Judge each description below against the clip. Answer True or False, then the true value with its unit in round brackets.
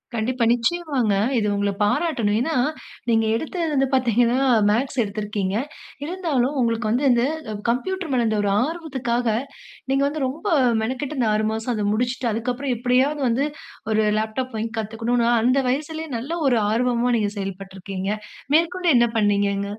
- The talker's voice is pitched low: False (240 Hz)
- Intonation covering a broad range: False (4.0 semitones)